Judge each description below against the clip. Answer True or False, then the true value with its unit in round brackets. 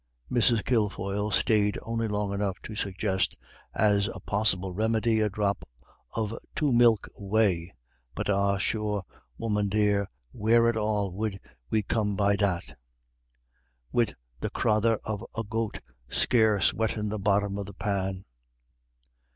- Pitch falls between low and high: False (105 Hz)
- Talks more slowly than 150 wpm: True (135 wpm)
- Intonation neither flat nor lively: False (1.8 semitones)